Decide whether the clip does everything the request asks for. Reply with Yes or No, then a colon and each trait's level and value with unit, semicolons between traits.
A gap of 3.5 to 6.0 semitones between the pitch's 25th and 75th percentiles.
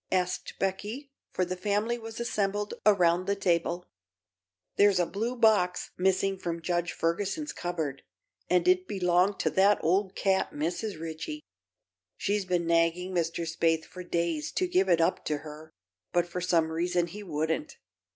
No: average, 3.1 semitones